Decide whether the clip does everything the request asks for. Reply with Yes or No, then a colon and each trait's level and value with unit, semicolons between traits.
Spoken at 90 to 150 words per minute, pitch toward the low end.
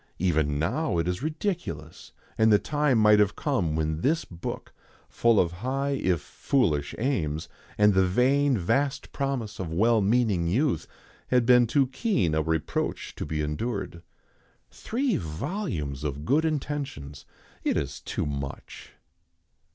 Yes: average, 145 wpm; low, 105 Hz